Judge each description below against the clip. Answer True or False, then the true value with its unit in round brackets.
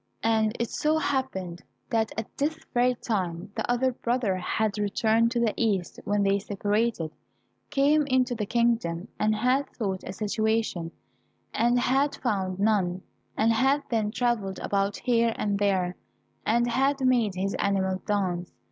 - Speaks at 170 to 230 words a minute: False (155 wpm)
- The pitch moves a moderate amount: True (3.7 semitones)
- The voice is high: True (220 Hz)